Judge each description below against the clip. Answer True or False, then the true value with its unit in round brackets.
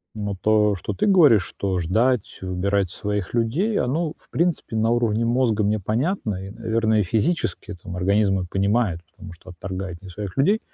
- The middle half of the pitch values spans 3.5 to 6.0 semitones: True (3.9 semitones)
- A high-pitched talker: False (105 Hz)